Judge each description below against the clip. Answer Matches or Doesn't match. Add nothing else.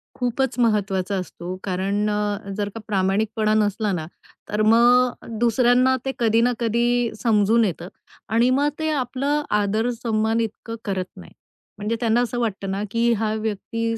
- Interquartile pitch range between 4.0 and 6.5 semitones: Doesn't match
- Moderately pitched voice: Doesn't match